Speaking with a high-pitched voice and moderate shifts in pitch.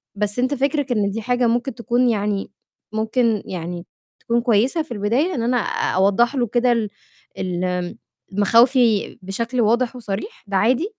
Yes: high, 230 Hz; average, 3.5 semitones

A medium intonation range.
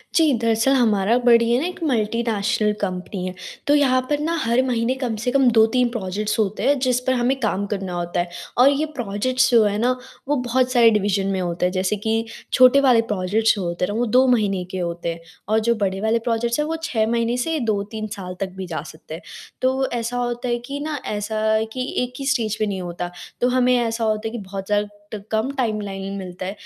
Yes: average, 4.1 semitones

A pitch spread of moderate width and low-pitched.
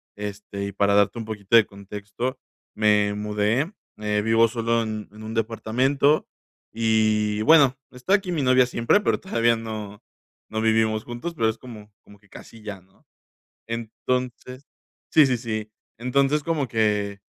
Yes: average, 3.2 semitones; low, 110 Hz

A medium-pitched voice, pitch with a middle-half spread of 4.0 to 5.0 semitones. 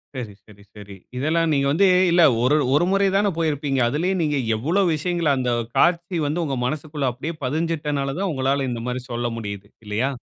Yes: medium, 145 Hz; average, 4.7 semitones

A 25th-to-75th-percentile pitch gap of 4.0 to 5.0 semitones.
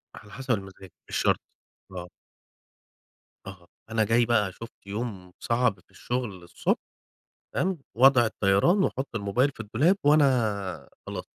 Yes: average, 4.6 semitones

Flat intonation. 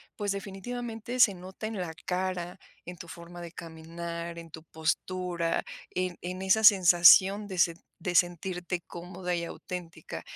Yes: narrow, 2.0 semitones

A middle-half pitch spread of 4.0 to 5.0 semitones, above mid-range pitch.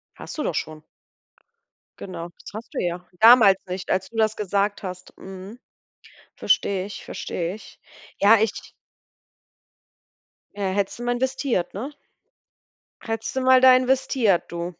Yes: average, 4.5 semitones; high, 205 Hz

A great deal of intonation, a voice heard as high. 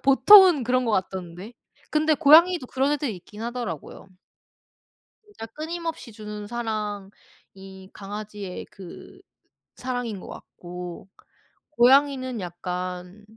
Yes: wide, 6.1 semitones; high, 225 Hz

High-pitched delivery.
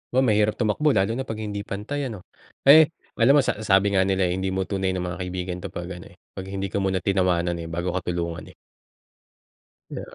No: very low, 95 Hz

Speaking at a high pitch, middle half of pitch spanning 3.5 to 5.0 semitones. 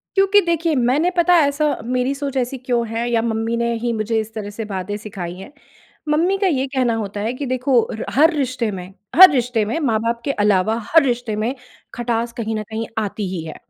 Yes: high, 235 Hz; average, 4.1 semitones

